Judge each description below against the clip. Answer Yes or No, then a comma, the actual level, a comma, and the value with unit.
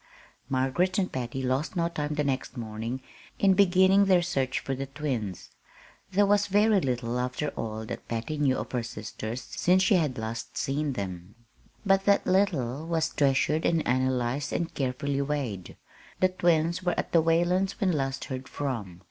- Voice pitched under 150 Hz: Yes, medium, 140 Hz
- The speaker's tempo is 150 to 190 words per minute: Yes, average, 170 wpm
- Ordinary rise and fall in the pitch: No, wide, 5.8 semitones